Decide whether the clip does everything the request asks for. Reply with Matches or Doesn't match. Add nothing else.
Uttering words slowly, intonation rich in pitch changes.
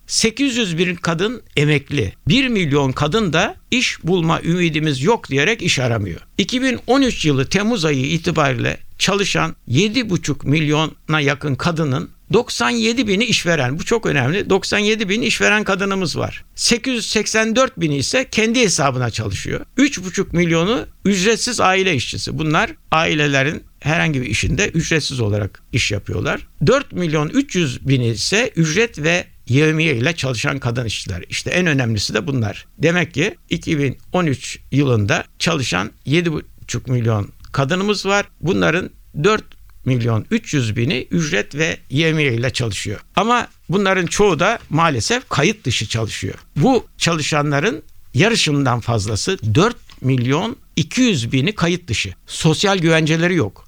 Doesn't match